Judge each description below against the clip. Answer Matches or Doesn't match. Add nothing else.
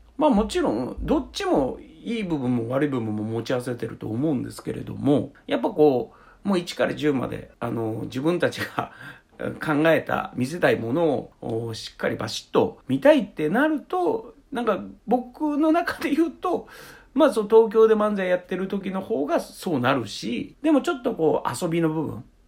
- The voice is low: Doesn't match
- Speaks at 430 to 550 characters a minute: Doesn't match